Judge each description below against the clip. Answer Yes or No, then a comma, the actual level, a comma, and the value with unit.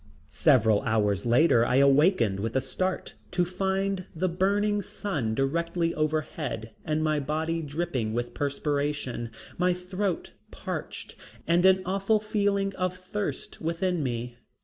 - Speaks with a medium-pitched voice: Yes, medium, 160 Hz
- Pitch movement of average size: No, wide, 6.0 semitones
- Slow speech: Yes, slow, 130 wpm